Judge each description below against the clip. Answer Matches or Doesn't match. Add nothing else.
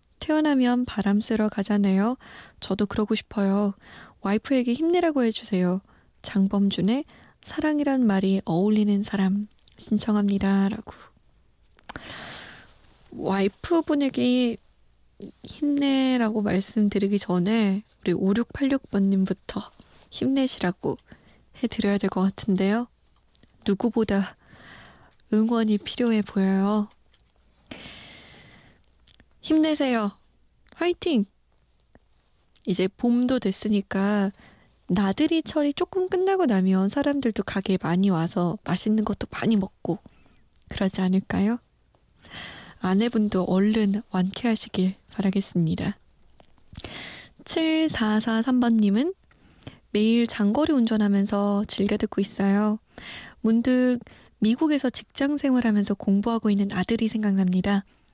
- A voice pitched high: Matches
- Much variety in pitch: Doesn't match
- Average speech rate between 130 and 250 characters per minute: Matches